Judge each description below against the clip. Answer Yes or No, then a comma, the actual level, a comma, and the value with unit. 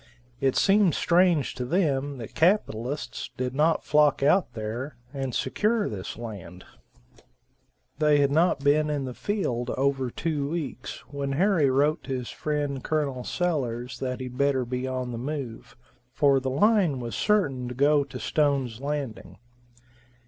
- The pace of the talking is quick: No, average, 150 wpm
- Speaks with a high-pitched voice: No, medium, 140 Hz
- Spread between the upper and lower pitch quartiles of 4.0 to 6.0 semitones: No, average, 3.2 semitones